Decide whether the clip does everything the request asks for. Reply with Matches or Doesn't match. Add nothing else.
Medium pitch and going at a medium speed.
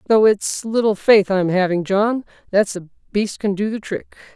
Doesn't match